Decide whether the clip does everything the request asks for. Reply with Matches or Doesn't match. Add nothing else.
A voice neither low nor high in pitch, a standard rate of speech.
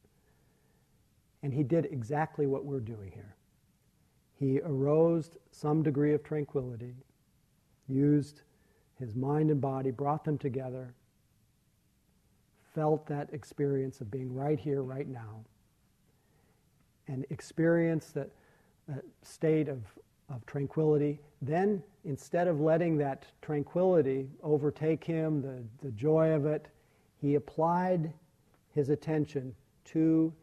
Doesn't match